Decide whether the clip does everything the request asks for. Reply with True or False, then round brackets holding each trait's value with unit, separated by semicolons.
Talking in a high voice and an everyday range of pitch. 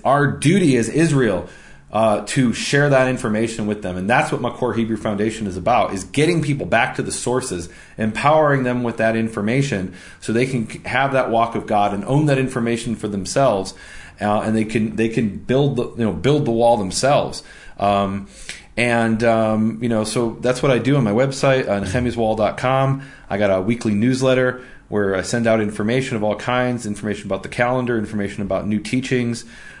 False (115 Hz; 3.4 semitones)